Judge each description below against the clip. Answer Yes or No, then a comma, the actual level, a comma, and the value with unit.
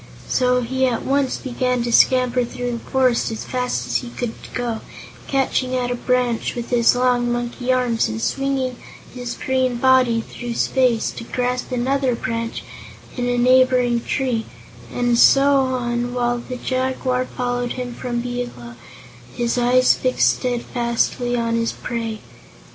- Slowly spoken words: No, average, 150 wpm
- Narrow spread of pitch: Yes, narrow, 1.1 semitones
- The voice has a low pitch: No, high, 245 Hz